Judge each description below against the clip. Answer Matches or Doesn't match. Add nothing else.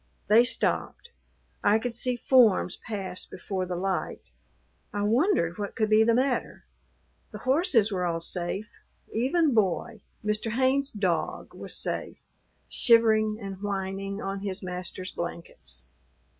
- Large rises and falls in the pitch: Doesn't match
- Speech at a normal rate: Doesn't match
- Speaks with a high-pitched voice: Matches